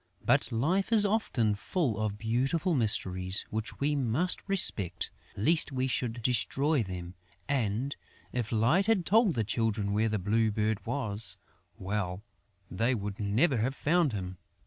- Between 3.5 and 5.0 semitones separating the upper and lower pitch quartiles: No, wide, 5.6 semitones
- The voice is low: Yes, low, 115 Hz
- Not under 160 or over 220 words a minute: No, average, 145 wpm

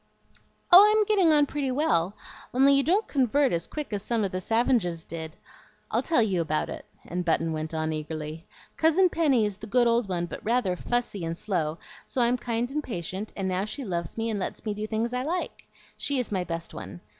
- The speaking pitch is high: Yes, high, 215 Hz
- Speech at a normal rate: No, fast, 215 wpm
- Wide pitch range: Yes, wide, 7.6 semitones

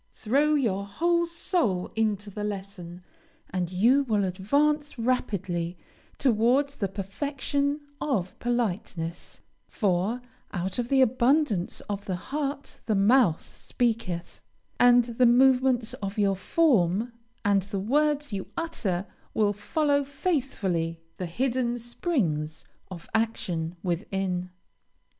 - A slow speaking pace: Yes, slow, 115 wpm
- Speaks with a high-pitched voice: Yes, high, 220 Hz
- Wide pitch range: Yes, wide, 6.0 semitones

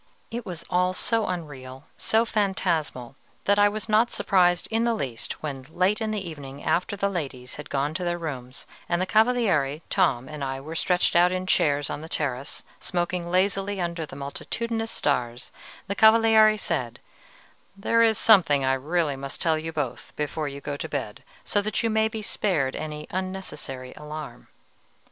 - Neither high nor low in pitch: Yes, medium, 170 Hz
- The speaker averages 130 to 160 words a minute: No, average, 175 wpm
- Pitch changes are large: Yes, wide, 6.2 semitones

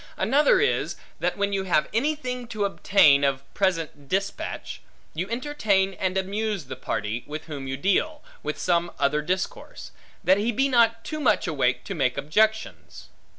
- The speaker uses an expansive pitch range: Yes, wide, 7.0 semitones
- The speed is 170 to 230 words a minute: No, average, 160 wpm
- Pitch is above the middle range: Yes, high, 195 Hz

